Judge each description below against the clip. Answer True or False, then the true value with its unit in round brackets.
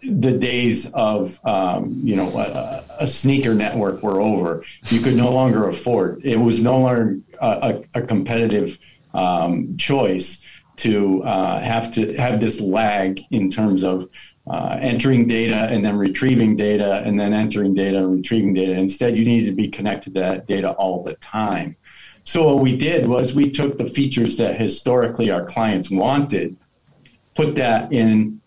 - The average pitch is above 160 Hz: False (115 Hz)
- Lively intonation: False (3.7 semitones)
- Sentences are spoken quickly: False (165 wpm)